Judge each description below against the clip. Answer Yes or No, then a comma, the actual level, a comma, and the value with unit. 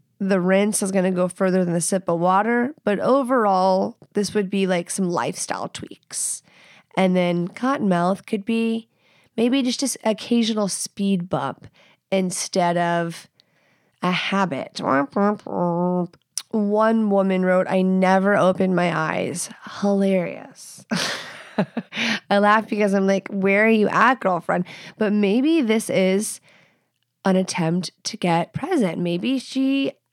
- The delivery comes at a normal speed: No, slow, 130 wpm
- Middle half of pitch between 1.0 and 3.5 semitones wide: Yes, average, 3.2 semitones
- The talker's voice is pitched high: Yes, high, 195 Hz